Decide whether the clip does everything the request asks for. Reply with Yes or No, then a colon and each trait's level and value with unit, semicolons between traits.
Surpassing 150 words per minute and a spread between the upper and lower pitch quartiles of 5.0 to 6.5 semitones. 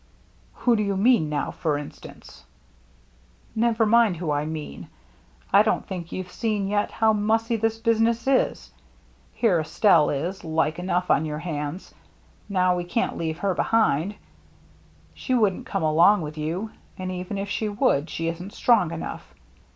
Yes: average, 165 wpm; wide, 5.5 semitones